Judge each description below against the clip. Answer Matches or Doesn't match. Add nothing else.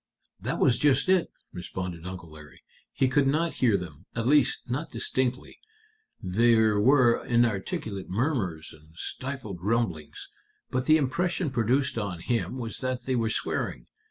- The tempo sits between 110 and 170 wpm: Matches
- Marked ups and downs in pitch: Matches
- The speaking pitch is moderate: Doesn't match